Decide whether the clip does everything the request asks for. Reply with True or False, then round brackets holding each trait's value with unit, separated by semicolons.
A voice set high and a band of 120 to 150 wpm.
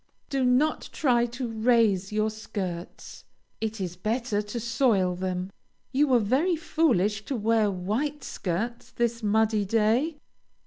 True (225 Hz; 135 wpm)